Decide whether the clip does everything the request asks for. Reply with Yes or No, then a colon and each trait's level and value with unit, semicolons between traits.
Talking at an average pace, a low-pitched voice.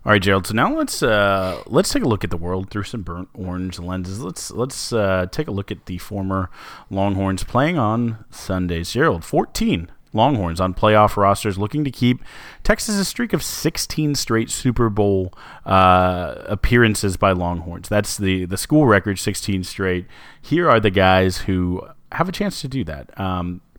Yes: average, 180 wpm; low, 100 Hz